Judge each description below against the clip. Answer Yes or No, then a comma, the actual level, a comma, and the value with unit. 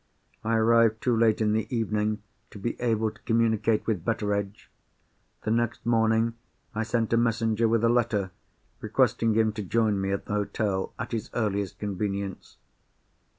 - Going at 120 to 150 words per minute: No, average, 160 wpm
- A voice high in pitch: No, low, 110 Hz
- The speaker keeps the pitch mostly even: Yes, narrow, 1.7 semitones